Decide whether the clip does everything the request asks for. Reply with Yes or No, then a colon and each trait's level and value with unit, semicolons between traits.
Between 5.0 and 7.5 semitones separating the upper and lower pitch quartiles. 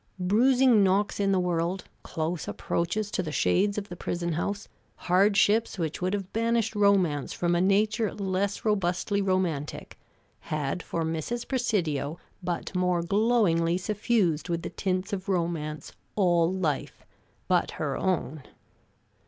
No: average, 3.3 semitones